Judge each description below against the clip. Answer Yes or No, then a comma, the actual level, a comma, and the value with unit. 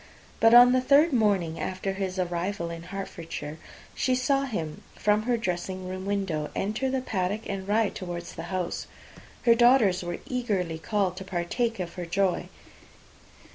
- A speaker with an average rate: Yes, average, 160 wpm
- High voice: Yes, high, 195 Hz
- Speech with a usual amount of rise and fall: Yes, average, 4.5 semitones